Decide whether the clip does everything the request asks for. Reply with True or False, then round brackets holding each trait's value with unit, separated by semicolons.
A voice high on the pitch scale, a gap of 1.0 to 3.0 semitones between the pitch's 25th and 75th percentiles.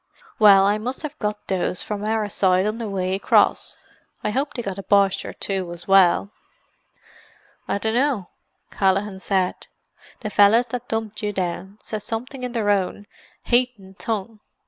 True (205 Hz; 2.6 semitones)